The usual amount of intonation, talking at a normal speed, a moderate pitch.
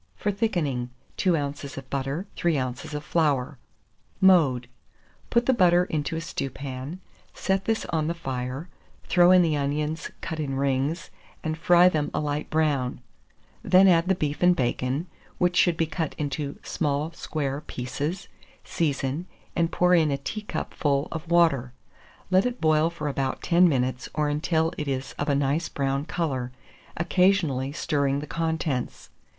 Yes: average, 3.8 semitones; average, 155 wpm; medium, 150 Hz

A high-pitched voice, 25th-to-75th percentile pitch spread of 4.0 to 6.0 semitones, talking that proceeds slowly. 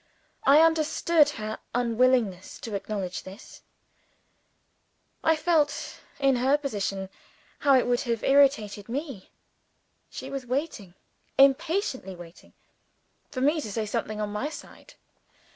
Yes: very high, 255 Hz; wide, 5.6 semitones; slow, 120 wpm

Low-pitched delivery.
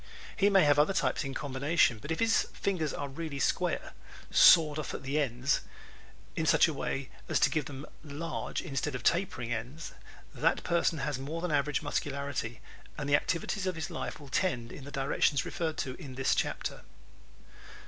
No: medium, 145 Hz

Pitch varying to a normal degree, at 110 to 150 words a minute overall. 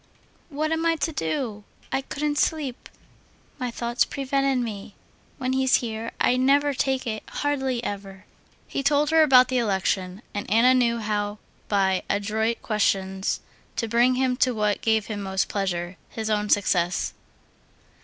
Yes: average, 4.5 semitones; average, 145 wpm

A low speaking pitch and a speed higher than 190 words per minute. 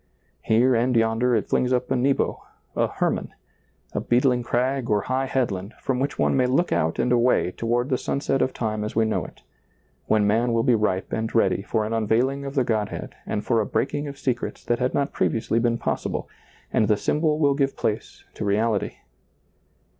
Yes: low, 120 Hz; average, 200 wpm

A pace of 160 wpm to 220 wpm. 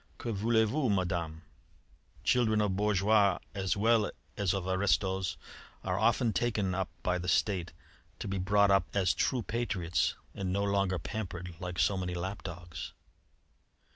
No: average, 150 wpm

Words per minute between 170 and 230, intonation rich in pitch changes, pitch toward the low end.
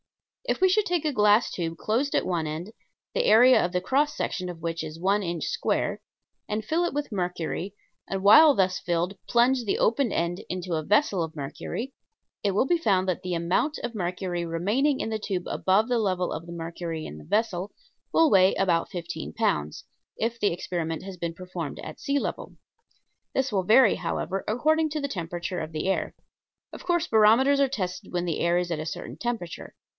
No: average, 200 wpm; wide, 5.8 semitones; high, 190 Hz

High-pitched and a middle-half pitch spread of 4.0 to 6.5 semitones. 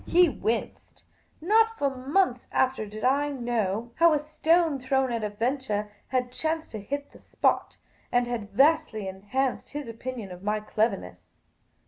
Yes: very high, 255 Hz; average, 5.2 semitones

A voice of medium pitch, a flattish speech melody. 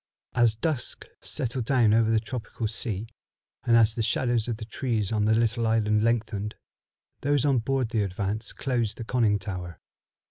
No: low, 115 Hz; narrow, 2.1 semitones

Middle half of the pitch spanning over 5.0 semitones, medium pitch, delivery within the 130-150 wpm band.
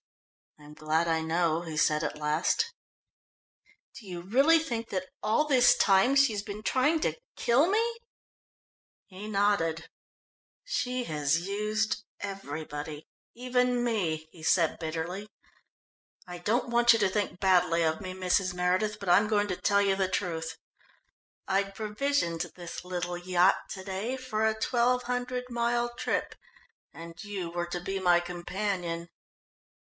No: wide, 5.4 semitones; high, 195 Hz; average, 145 wpm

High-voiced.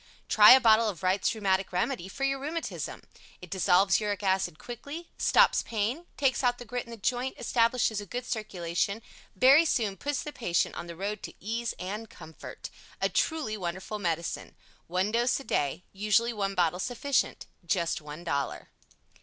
Yes: high, 210 Hz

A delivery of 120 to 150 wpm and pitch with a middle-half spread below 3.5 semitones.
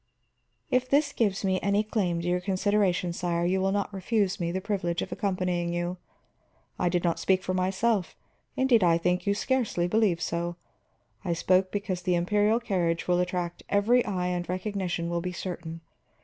No: average, 175 wpm; narrow, 2.6 semitones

